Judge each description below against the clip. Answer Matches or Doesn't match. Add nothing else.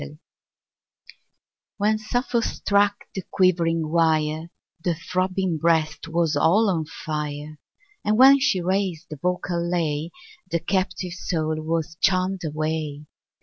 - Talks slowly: Matches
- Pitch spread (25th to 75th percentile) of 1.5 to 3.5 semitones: Matches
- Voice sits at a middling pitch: Matches